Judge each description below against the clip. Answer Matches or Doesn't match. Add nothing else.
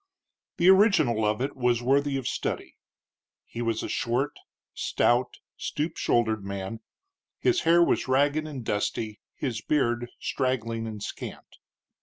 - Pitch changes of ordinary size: Matches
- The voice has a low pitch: Matches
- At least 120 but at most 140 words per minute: Matches